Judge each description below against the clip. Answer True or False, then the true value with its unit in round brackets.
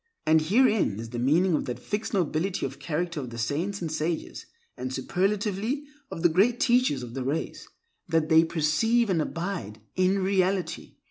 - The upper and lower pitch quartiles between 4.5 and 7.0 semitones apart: True (4.8 semitones)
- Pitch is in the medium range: True (170 Hz)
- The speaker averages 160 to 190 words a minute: True (165 wpm)